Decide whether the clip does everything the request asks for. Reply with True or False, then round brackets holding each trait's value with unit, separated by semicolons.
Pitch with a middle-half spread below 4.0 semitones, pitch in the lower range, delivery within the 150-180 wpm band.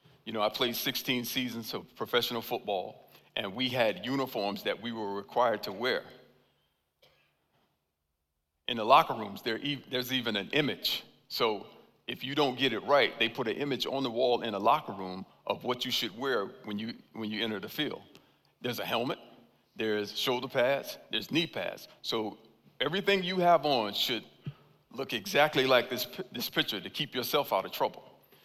False (4.5 semitones; 115 Hz; 175 wpm)